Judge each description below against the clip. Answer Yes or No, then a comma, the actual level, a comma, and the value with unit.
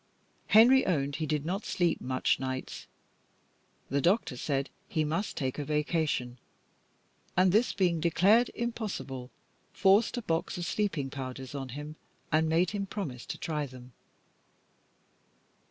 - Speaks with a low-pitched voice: No, medium, 155 Hz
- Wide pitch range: Yes, wide, 5.9 semitones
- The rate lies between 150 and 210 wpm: No, average, 140 wpm